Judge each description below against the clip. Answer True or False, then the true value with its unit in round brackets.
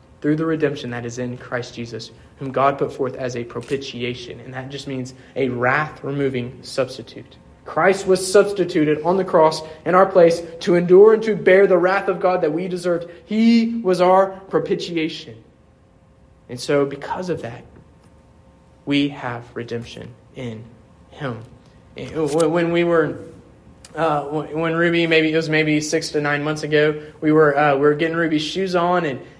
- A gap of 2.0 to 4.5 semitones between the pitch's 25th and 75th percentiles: False (5.1 semitones)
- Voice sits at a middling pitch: True (155 Hz)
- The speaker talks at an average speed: True (170 wpm)